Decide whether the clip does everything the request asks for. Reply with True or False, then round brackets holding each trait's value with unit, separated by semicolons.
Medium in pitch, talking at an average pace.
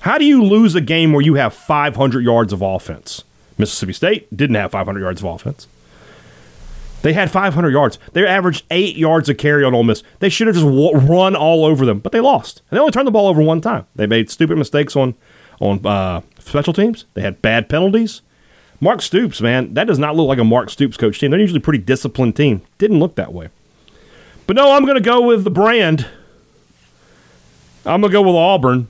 False (145 Hz; 220 wpm)